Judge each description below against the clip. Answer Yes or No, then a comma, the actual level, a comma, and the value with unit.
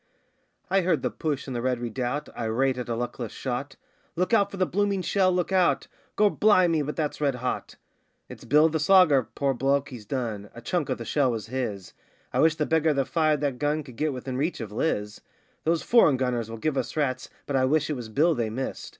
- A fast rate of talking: Yes, fast, 225 wpm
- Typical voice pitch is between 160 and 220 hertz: No, medium, 140 Hz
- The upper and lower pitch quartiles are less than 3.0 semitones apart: No, average, 4.5 semitones